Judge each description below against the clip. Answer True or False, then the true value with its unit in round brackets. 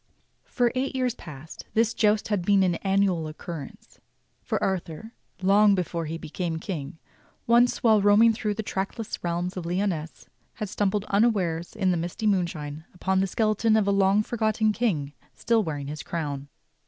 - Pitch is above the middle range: True (195 Hz)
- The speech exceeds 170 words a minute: False (165 wpm)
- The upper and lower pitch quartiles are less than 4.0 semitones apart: False (4.3 semitones)